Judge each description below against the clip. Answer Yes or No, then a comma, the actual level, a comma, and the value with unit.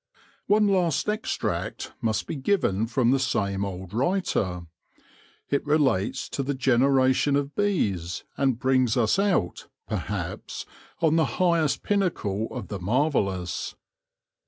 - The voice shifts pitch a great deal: Yes, wide, 7.5 semitones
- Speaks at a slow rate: Yes, slow, 130 wpm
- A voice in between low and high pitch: No, low, 130 Hz